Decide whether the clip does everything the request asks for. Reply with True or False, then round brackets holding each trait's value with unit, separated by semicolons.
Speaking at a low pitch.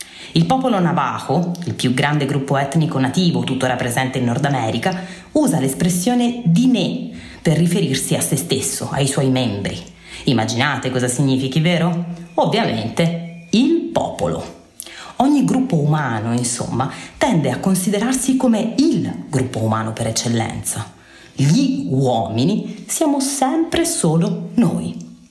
False (165 Hz)